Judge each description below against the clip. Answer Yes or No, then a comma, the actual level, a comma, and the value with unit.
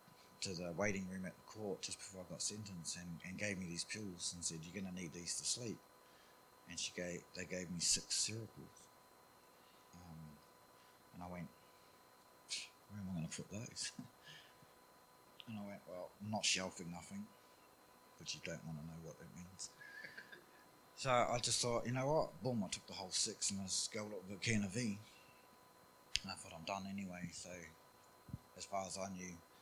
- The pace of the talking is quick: No, average, 195 wpm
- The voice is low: Yes, very low, 90 Hz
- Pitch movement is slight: No, average, 3.2 semitones